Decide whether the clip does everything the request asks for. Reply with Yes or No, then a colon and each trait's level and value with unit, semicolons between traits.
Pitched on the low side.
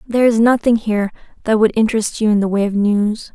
No: high, 215 Hz